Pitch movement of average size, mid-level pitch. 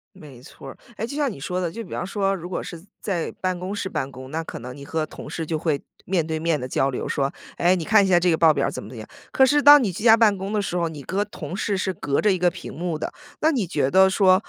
Yes: average, 4.2 semitones; medium, 180 Hz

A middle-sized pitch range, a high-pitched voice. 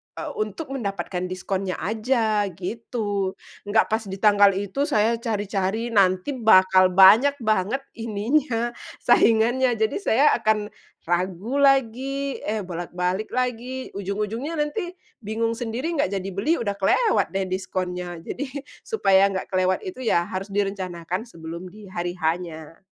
Yes: average, 4.1 semitones; high, 205 Hz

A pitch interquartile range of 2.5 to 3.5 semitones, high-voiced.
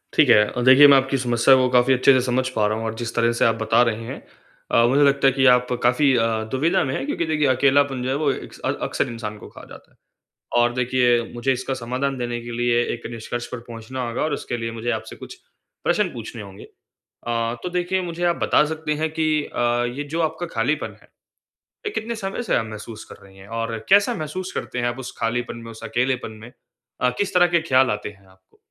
No: average, 3.2 semitones; low, 125 Hz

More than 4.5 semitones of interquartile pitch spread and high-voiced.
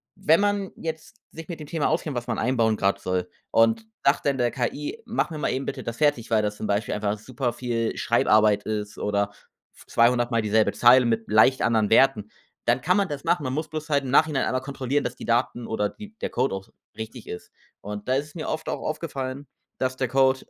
No: average, 4.9 semitones; low, 130 Hz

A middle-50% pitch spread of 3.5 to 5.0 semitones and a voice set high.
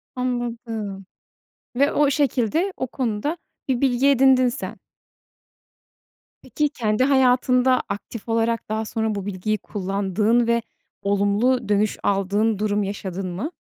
Yes: average, 3.9 semitones; high, 230 Hz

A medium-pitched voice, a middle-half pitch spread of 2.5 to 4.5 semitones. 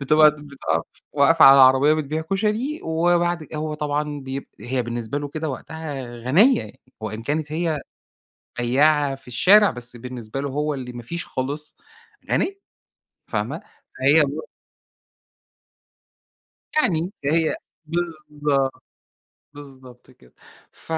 Yes: medium, 145 Hz; average, 3.4 semitones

